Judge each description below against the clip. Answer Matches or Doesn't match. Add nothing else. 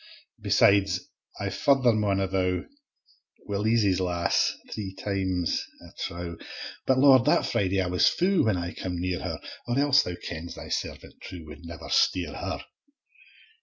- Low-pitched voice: Matches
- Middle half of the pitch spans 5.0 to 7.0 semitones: Doesn't match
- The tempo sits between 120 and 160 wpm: Matches